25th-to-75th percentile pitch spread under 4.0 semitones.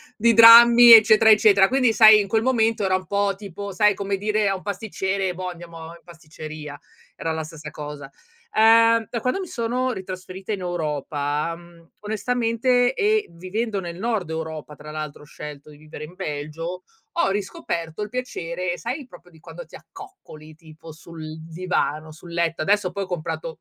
No: wide, 5.5 semitones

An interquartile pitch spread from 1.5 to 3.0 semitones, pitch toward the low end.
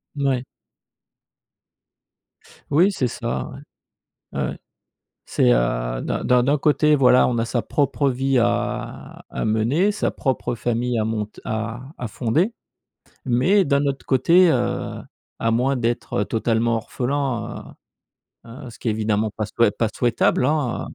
No: average, 3.5 semitones; low, 125 Hz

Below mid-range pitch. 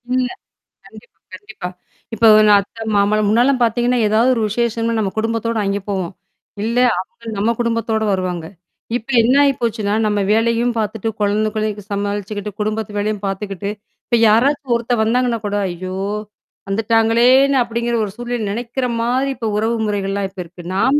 No: high, 220 Hz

